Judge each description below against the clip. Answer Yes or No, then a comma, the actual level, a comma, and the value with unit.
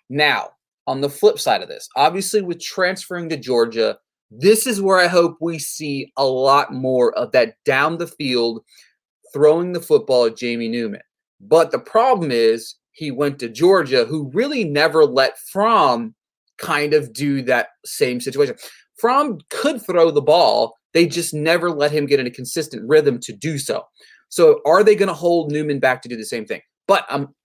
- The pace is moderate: Yes, average, 190 wpm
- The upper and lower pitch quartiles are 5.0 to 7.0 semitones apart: Yes, wide, 5.5 semitones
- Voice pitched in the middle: Yes, medium, 155 Hz